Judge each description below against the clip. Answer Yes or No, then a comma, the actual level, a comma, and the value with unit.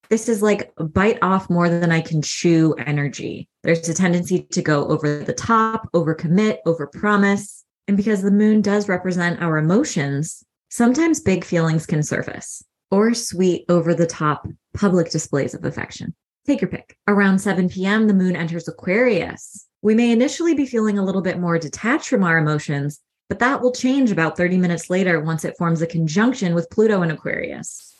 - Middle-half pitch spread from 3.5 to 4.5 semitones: Yes, average, 4.1 semitones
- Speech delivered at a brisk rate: No, average, 185 wpm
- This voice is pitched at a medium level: Yes, medium, 180 Hz